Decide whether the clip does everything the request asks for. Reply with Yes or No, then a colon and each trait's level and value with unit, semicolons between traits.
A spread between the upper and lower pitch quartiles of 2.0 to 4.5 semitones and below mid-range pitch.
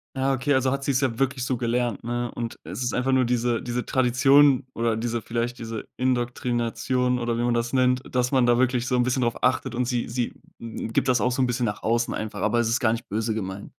No: narrow, 1.6 semitones; low, 120 Hz